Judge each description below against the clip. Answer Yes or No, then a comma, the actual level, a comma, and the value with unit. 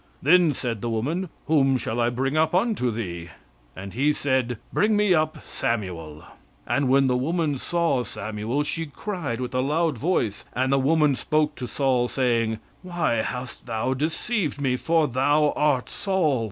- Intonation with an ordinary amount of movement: Yes, average, 4.6 semitones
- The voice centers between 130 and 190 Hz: Yes, low, 135 Hz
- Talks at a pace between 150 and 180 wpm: Yes, average, 165 wpm